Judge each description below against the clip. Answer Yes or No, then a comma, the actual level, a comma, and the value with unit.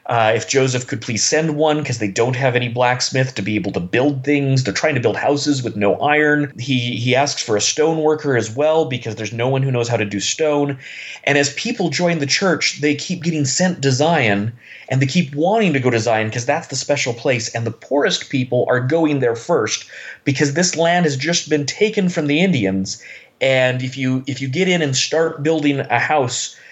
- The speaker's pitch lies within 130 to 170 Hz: Yes, low, 135 Hz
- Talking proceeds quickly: Yes, fast, 225 wpm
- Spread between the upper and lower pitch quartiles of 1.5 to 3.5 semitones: No, average, 3.9 semitones